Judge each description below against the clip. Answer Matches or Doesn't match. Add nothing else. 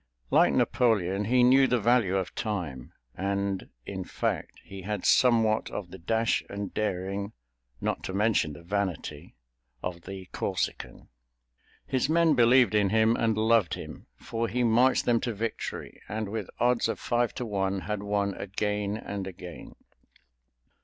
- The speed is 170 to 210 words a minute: Doesn't match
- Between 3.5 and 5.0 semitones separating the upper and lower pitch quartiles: Doesn't match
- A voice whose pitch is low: Matches